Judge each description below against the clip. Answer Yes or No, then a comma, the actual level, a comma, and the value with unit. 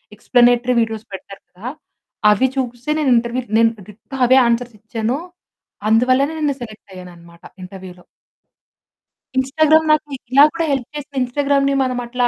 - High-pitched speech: Yes, high, 245 Hz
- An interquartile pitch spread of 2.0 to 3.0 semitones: No, average, 3.7 semitones